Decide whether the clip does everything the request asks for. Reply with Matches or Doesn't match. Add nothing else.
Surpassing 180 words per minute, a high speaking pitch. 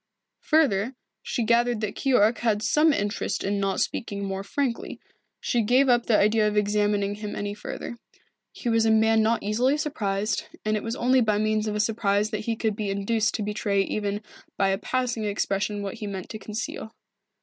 Matches